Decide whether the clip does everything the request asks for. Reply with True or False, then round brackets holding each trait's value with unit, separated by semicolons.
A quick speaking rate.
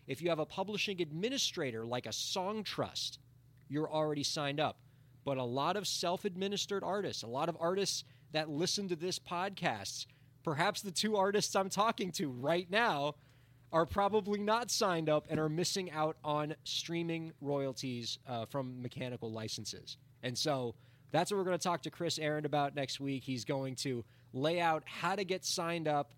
False (180 wpm)